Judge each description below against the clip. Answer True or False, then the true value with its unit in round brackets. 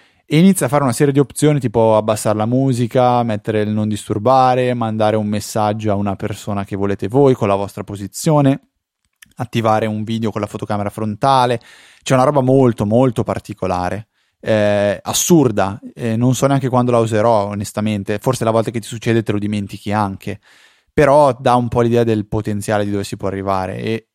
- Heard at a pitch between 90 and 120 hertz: True (110 Hz)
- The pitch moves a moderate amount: True (3.3 semitones)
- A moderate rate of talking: False (185 wpm)